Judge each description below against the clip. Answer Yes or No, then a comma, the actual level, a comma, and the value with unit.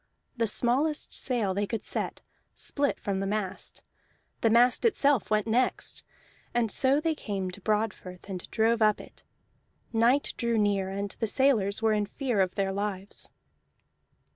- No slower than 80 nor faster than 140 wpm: No, average, 155 wpm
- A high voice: Yes, high, 215 Hz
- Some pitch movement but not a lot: Yes, average, 3.4 semitones